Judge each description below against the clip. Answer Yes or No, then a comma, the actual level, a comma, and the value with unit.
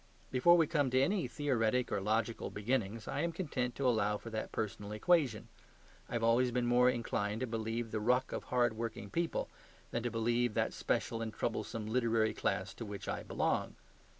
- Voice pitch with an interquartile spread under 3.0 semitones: Yes, narrow, 2.5 semitones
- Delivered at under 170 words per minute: No, average, 190 wpm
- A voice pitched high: No, low, 115 Hz